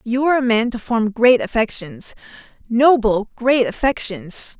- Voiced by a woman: Yes, female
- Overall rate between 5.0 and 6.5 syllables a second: No, 4.4 syllables/s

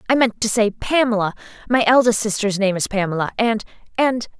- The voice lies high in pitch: Yes, high, 220 Hz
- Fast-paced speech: No, average, 165 wpm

